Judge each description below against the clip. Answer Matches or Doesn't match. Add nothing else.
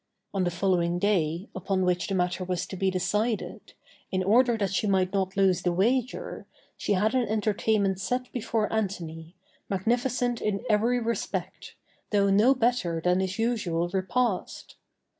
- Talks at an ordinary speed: Matches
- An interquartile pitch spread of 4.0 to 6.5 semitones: Doesn't match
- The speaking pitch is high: Matches